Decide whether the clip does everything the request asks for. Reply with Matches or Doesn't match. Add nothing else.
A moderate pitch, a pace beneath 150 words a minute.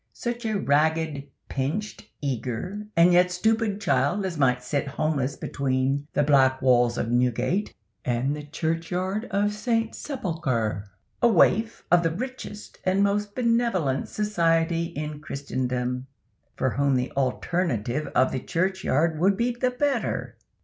Matches